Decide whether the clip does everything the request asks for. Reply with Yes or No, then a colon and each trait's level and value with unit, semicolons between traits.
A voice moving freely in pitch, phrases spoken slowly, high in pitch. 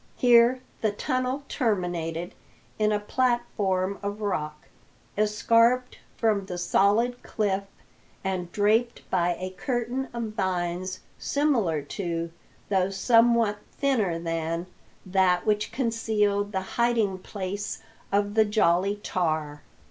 No: average, 4.1 semitones; slow, 110 wpm; high, 205 Hz